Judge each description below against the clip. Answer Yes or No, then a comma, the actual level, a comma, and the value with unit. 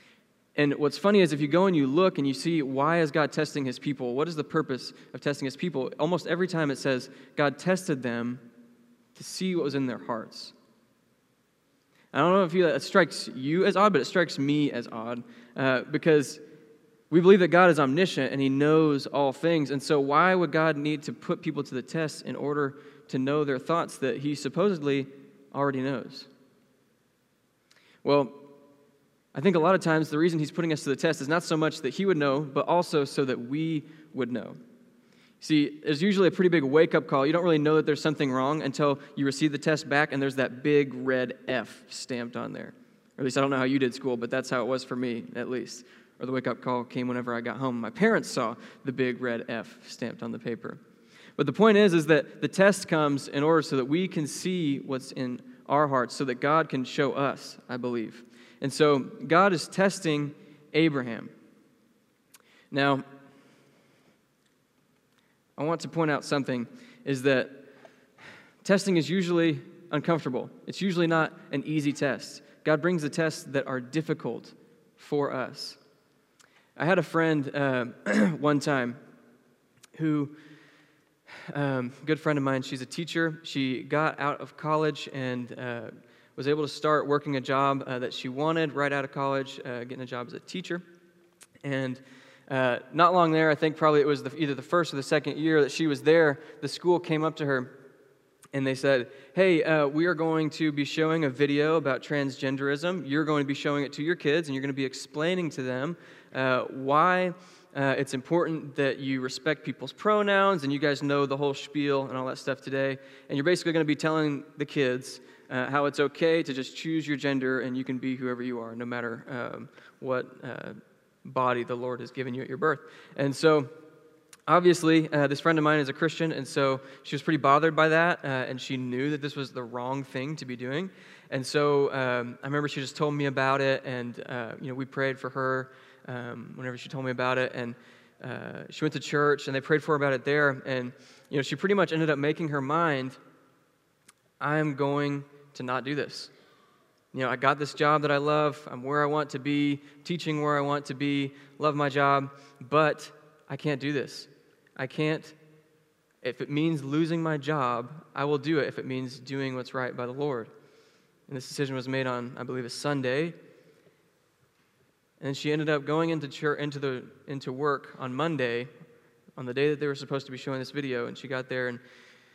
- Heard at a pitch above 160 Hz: No, medium, 145 Hz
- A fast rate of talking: Yes, fast, 210 wpm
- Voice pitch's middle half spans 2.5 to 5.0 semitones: Yes, average, 2.9 semitones